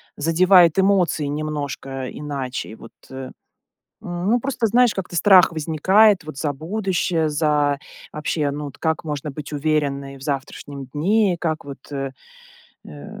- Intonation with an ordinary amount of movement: Yes, average, 4.1 semitones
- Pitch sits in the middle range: Yes, medium, 155 Hz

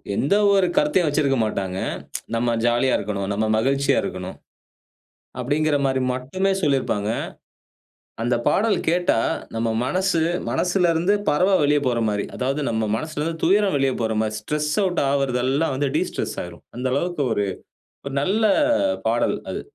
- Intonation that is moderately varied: No, wide, 5.7 semitones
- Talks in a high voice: No, medium, 140 Hz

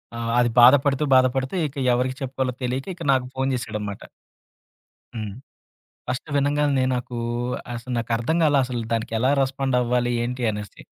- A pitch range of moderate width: No, narrow, 2.0 semitones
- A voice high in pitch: No, low, 125 Hz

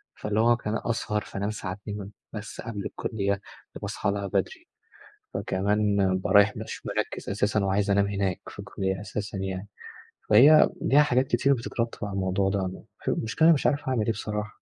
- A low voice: Yes, low, 105 Hz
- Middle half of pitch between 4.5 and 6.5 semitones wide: No, narrow, 2.5 semitones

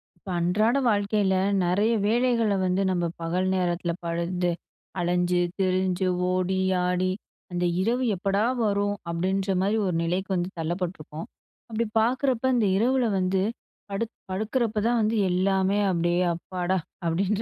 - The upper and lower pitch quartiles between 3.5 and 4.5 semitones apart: No, average, 3.0 semitones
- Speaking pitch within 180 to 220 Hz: Yes, high, 190 Hz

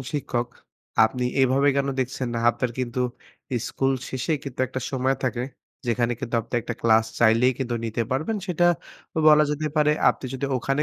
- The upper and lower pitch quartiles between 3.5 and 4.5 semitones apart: No, narrow, 2.6 semitones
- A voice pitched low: Yes, low, 130 Hz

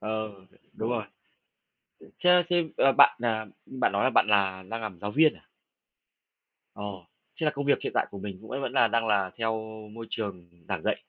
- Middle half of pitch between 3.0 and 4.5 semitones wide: No, average, 4.9 semitones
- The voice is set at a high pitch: No, low, 110 Hz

